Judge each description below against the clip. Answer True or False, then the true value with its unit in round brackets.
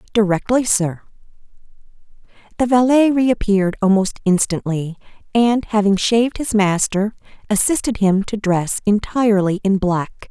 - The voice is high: True (210 Hz)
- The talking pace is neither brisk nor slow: False (115 wpm)